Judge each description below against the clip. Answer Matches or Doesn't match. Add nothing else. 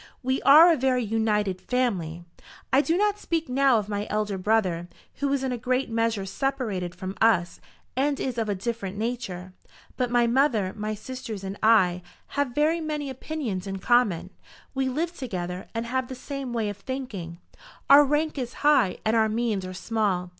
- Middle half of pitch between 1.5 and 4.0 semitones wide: Doesn't match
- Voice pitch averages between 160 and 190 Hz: Doesn't match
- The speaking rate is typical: Matches